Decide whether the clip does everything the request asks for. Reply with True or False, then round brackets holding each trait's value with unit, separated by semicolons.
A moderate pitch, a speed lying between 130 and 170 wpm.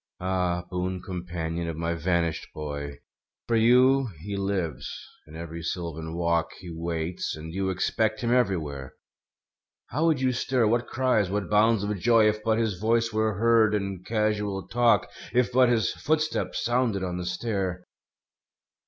False (100 Hz; 155 wpm)